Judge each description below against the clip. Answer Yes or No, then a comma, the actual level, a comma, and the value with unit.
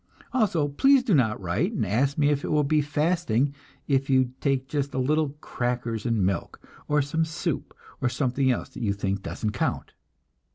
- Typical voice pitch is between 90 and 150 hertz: Yes, low, 135 Hz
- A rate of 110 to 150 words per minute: No, average, 190 wpm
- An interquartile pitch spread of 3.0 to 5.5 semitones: Yes, average, 3.9 semitones